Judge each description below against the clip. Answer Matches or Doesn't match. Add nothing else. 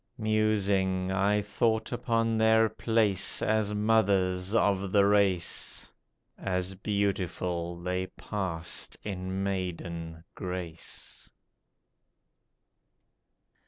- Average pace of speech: Doesn't match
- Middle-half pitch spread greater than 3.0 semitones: Doesn't match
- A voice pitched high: Doesn't match